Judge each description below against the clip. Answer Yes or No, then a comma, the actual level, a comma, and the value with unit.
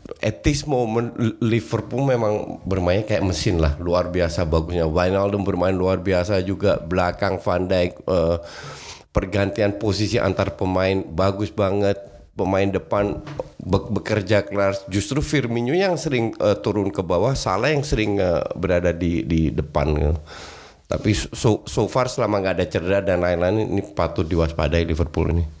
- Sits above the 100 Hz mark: No, very low, 95 Hz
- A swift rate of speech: Yes, fast, 150 wpm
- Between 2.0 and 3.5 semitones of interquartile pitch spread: Yes, average, 3.1 semitones